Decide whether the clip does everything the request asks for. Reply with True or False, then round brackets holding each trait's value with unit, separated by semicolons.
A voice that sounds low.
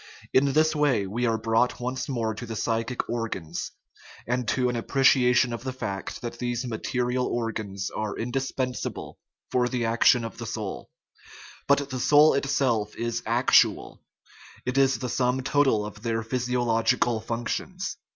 True (120 Hz)